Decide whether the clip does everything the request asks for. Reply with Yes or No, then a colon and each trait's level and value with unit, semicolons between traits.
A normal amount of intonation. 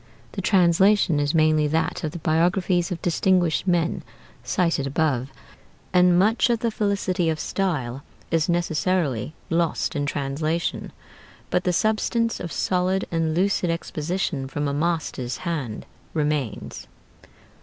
Yes: average, 3.4 semitones